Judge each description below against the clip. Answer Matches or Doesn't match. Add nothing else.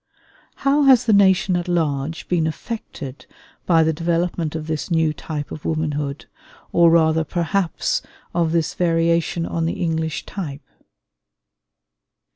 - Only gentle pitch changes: Matches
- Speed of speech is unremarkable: Doesn't match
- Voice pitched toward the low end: Doesn't match